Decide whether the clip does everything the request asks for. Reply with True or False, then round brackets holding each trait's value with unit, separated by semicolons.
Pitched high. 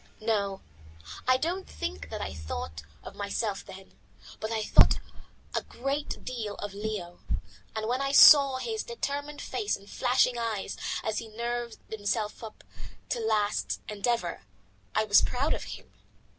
True (220 Hz)